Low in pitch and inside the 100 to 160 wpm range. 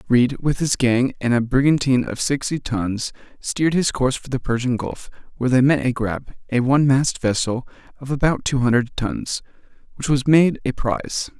No: low, 130 Hz; average, 190 wpm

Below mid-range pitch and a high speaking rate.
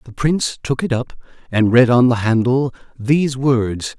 No: low, 125 Hz; average, 180 wpm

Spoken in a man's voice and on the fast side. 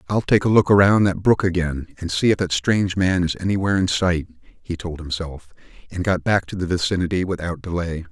Yes: male; fast, 215 wpm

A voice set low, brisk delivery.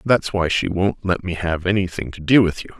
Yes: very low, 90 Hz; fast, 260 wpm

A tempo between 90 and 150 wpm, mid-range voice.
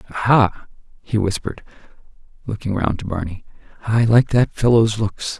No: slow, 135 wpm; low, 105 Hz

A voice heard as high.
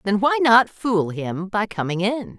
Yes: high, 210 Hz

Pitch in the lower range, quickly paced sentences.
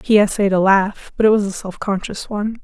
No: high, 200 Hz; fast, 250 wpm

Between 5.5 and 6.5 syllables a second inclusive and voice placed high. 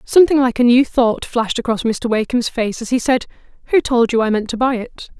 Yes: 5.7 syllables/s; high, 240 Hz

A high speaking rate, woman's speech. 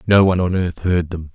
No: fast, 265 wpm; male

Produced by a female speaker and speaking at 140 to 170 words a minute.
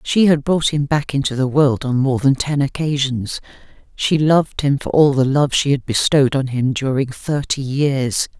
No: female; average, 200 wpm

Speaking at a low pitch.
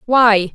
No: high, 220 Hz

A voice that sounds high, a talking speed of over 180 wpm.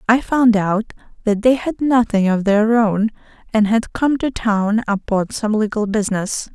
No: high, 220 Hz; average, 175 wpm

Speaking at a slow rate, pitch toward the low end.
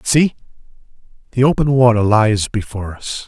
Yes: slow, 130 wpm; low, 115 Hz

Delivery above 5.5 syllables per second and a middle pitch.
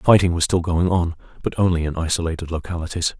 No: 6.3 syllables/s; very low, 85 Hz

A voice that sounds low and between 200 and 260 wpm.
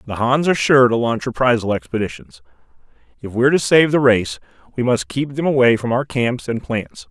Yes: low, 120 Hz; fast, 205 wpm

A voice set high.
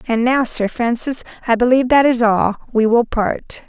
Yes: high, 240 Hz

